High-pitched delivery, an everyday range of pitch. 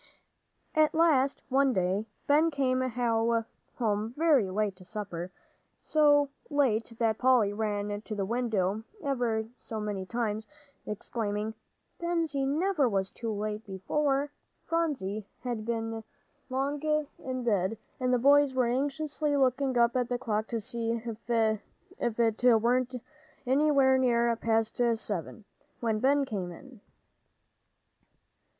Yes: high, 235 Hz; average, 4.2 semitones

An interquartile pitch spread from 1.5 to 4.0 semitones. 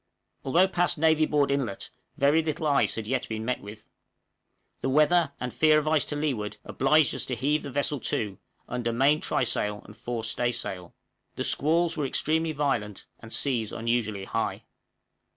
No: average, 5.2 semitones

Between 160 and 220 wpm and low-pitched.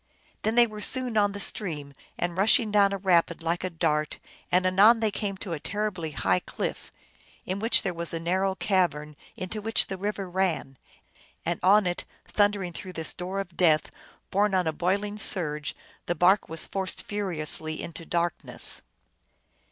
No: average, 175 wpm; medium, 185 Hz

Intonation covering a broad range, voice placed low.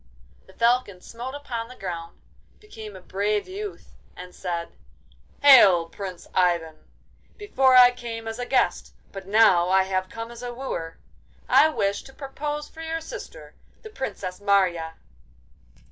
No: wide, 6.0 semitones; high, 225 Hz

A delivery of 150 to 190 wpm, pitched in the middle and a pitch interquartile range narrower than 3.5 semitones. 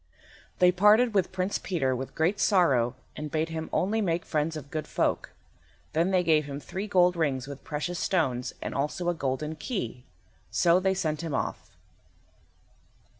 No: average, 170 wpm; medium, 165 Hz; average, 4.1 semitones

